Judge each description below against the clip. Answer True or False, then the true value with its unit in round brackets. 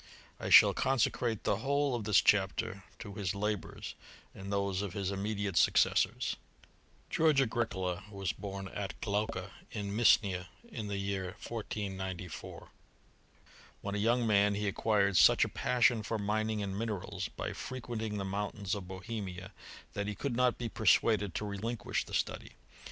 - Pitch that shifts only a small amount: True (2.3 semitones)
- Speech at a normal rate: True (155 wpm)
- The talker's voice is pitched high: False (100 Hz)